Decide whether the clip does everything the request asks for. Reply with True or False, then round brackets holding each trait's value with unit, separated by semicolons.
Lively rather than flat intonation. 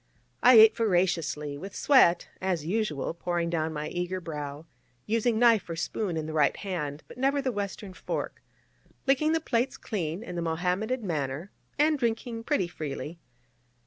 True (6.0 semitones)